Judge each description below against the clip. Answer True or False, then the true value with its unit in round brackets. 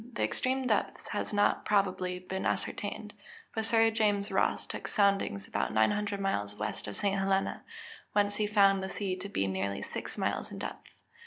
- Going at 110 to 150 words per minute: False (180 wpm)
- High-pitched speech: True (200 Hz)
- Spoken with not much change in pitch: True (2.3 semitones)